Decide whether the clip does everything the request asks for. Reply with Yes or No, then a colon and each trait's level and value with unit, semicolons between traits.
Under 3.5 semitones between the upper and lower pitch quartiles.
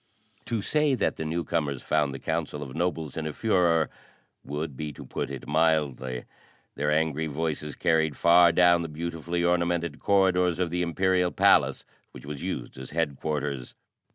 Yes: average, 2.8 semitones